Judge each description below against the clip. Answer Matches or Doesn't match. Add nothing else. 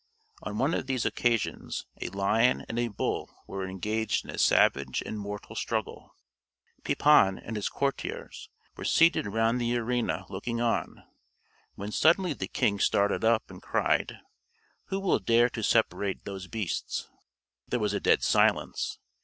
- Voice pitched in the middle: Doesn't match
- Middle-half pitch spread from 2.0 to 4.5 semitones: Matches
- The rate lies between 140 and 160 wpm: Matches